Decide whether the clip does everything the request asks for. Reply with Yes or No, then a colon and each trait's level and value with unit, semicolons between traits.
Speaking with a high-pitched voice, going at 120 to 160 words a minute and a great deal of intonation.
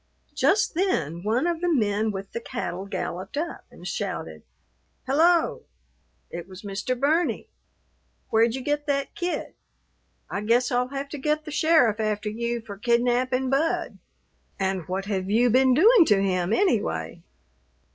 Yes: high, 240 Hz; average, 150 wpm; wide, 6.5 semitones